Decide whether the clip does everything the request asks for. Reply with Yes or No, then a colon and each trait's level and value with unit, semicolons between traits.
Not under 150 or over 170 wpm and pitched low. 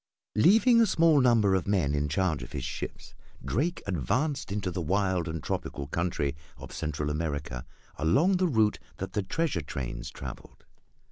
Yes: average, 160 wpm; very low, 95 Hz